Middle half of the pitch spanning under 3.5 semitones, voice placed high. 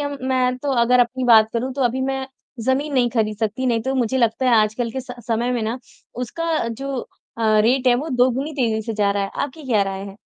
Yes: average, 2.8 semitones; high, 245 Hz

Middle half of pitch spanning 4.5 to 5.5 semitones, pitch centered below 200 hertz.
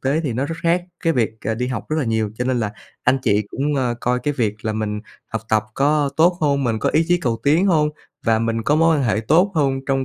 Yes: average, 5.2 semitones; low, 135 Hz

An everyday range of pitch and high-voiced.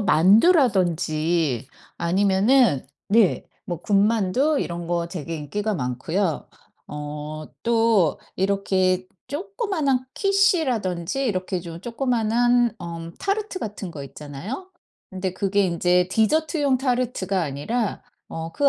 No: wide, 6.5 semitones; high, 195 Hz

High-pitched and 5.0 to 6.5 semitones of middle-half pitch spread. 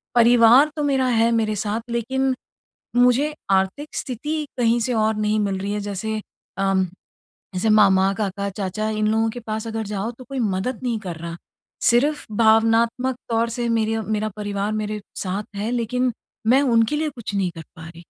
No: high, 220 Hz; average, 3.0 semitones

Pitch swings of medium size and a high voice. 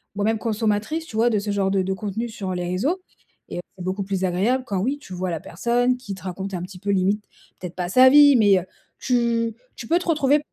Yes: average, 4.5 semitones; high, 205 Hz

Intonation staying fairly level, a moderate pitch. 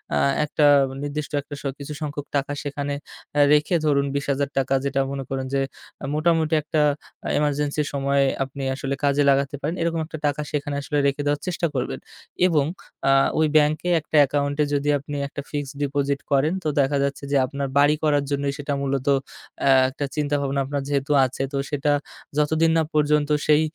Yes: narrow, 1.3 semitones; medium, 145 Hz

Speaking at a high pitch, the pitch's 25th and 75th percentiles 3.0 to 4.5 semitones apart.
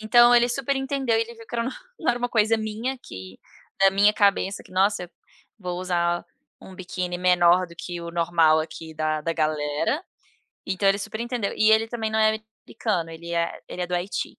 No: high, 195 Hz; average, 4.9 semitones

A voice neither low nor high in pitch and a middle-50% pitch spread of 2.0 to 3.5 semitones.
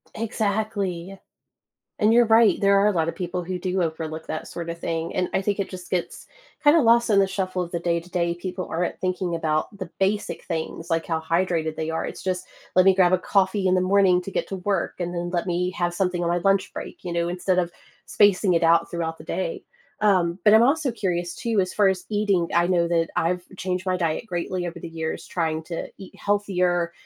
Yes: medium, 180 Hz; narrow, 2.4 semitones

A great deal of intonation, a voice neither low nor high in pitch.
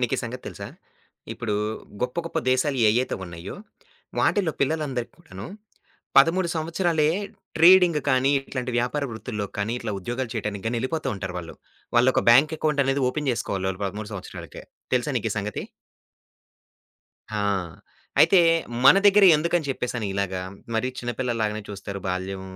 No: wide, 6.2 semitones; low, 125 Hz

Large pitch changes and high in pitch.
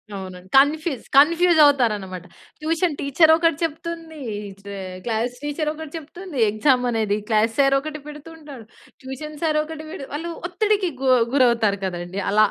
Yes: wide, 6.1 semitones; very high, 290 Hz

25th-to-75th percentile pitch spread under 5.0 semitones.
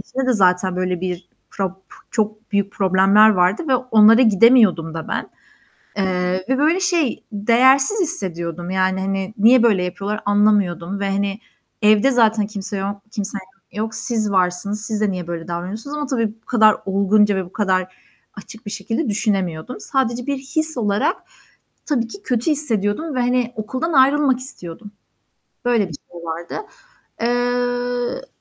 Yes: average, 4.5 semitones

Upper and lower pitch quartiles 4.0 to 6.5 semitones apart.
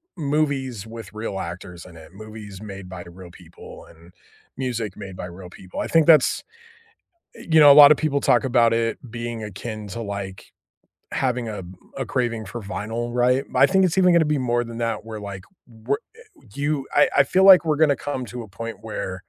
Yes: wide, 5.6 semitones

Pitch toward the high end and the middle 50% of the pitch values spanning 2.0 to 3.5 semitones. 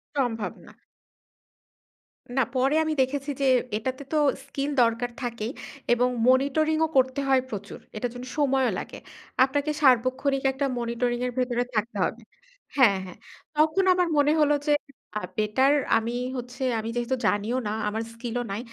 Yes: very high, 255 Hz; average, 3.0 semitones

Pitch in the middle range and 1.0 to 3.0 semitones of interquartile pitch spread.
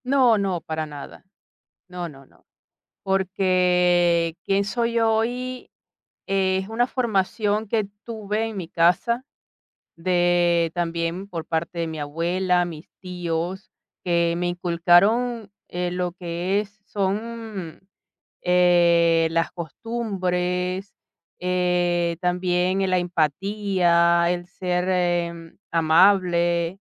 Yes: medium, 180 Hz; narrow, 2.5 semitones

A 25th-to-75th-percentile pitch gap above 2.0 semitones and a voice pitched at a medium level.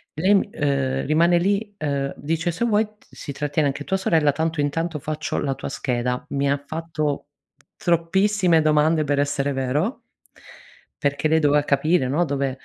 Yes: average, 2.9 semitones; medium, 150 Hz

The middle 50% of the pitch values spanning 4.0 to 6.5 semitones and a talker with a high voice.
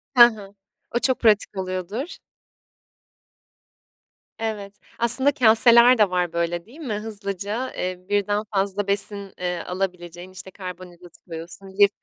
No: average, 3.4 semitones; high, 200 Hz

